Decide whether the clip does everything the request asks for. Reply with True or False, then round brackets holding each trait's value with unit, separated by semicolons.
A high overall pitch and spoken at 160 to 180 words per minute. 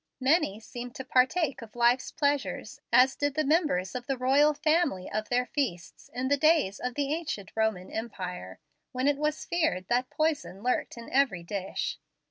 True (255 Hz; 175 wpm)